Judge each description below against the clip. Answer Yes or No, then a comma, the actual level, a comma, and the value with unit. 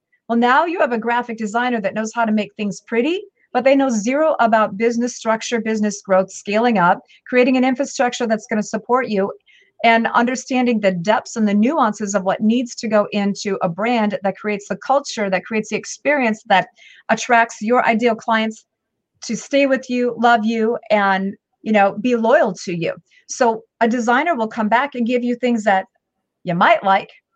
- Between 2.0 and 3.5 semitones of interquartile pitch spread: Yes, average, 2.9 semitones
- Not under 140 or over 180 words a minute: No, average, 195 wpm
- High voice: Yes, high, 230 Hz